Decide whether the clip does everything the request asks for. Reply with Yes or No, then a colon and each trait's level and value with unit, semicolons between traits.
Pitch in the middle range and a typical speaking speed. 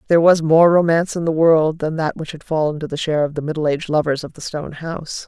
No: medium, 160 Hz; fast, 275 wpm